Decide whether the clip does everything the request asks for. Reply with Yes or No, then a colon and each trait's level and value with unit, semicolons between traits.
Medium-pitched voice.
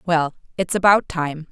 Yes: medium, 170 Hz